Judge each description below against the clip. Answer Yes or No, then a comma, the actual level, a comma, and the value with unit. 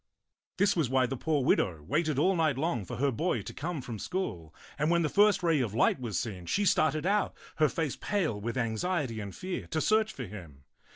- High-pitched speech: No, medium, 145 Hz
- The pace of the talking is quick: Yes, fast, 220 wpm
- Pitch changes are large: Yes, wide, 7.3 semitones